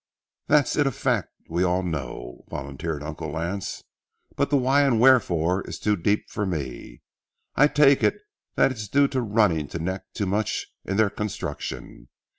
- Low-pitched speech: Yes, low, 100 Hz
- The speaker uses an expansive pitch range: Yes, wide, 7.6 semitones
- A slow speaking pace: No, average, 170 wpm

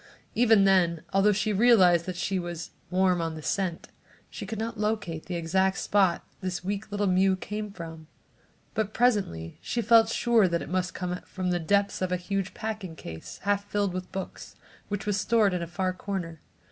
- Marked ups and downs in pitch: No, average, 2.8 semitones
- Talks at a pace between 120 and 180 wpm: No, average, 190 wpm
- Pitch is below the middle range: No, high, 190 Hz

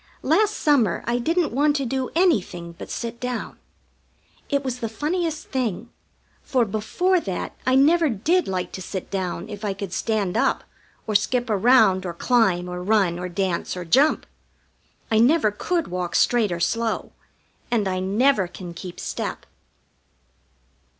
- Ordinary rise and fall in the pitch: No, wide, 6.2 semitones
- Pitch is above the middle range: Yes, high, 220 Hz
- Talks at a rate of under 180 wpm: Yes, average, 155 wpm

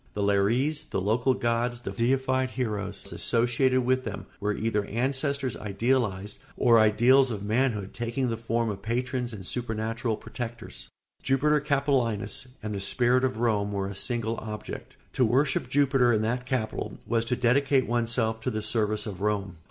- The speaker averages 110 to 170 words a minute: Yes, average, 160 wpm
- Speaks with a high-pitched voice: No, low, 115 Hz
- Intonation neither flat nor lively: Yes, average, 3.1 semitones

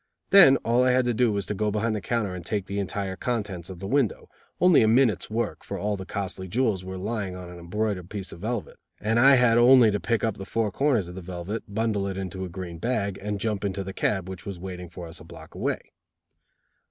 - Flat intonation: No, average, 3.5 semitones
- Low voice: Yes, low, 100 Hz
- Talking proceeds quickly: Yes, fast, 245 wpm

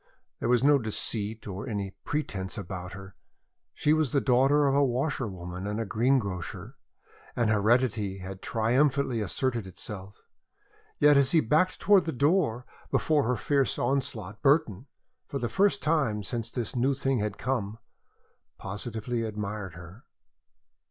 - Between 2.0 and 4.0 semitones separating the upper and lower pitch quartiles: No, average, 5.3 semitones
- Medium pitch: No, low, 115 Hz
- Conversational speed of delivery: Yes, average, 145 wpm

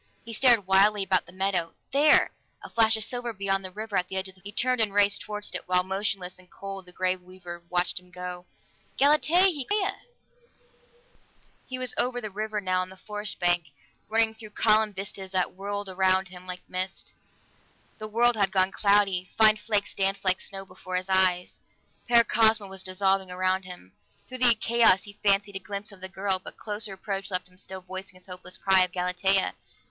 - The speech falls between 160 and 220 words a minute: Yes, average, 200 wpm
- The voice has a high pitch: Yes, high, 195 Hz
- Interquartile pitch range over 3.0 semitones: No, narrow, 2.6 semitones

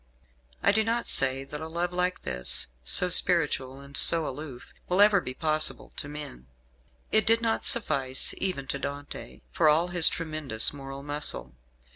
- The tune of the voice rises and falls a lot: No, average, 4.6 semitones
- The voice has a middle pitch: Yes, medium, 155 Hz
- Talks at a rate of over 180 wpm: No, average, 165 wpm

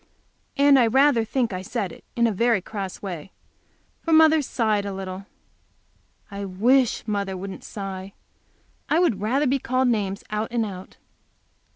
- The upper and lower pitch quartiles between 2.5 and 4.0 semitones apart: No, average, 4.8 semitones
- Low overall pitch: No, high, 215 Hz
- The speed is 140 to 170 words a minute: Yes, average, 160 wpm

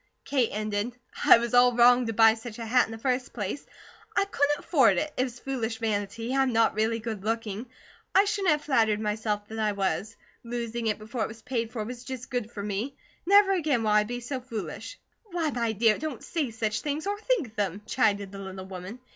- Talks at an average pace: No, fast, 215 wpm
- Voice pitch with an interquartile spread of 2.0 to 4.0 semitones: Yes, average, 3.4 semitones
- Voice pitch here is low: No, high, 230 Hz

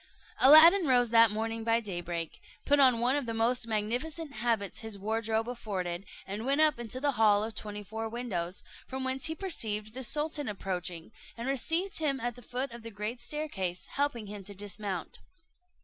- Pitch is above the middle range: Yes, high, 230 Hz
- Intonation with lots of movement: No, average, 4.1 semitones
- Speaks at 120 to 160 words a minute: No, average, 180 wpm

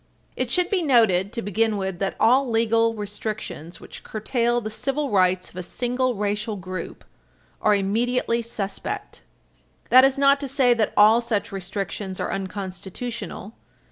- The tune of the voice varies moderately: Yes, average, 3.9 semitones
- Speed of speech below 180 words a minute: Yes, average, 150 wpm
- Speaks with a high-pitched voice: Yes, high, 220 Hz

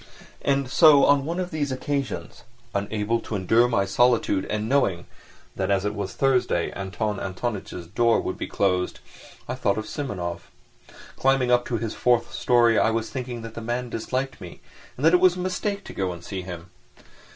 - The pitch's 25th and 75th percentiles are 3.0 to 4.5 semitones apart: No, average, 5.1 semitones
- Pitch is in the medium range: No, low, 115 Hz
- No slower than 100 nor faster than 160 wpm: No, average, 180 wpm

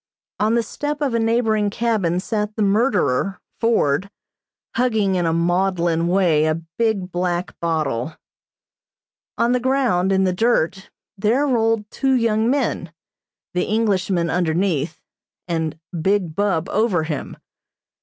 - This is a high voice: Yes, high, 195 Hz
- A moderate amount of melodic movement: Yes, average, 4.9 semitones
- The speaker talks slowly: Yes, slow, 130 wpm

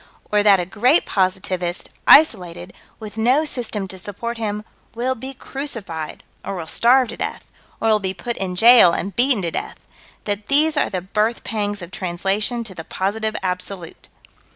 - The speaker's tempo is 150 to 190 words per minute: Yes, average, 175 wpm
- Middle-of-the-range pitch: No, high, 210 Hz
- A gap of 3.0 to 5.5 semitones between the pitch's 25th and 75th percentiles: Yes, average, 4.2 semitones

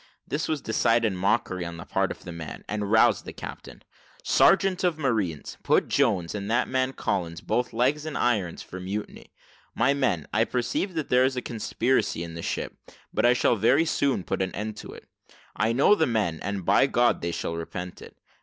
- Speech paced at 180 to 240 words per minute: Yes, average, 200 wpm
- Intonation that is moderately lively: No, wide, 6.2 semitones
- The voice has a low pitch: Yes, low, 110 Hz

